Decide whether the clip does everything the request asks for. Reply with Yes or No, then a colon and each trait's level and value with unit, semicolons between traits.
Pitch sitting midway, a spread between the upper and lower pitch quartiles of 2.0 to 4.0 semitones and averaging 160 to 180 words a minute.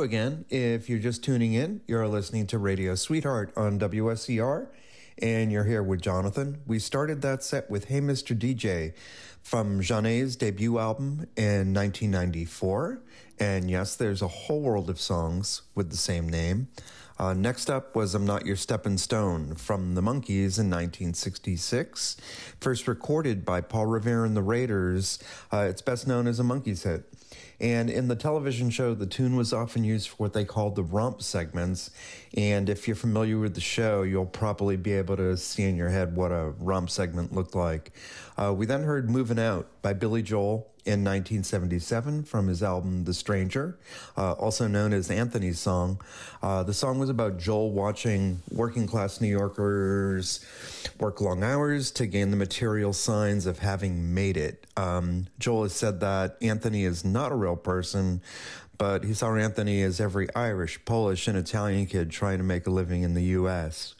No: low, 105 Hz; average, 3.5 semitones; average, 175 wpm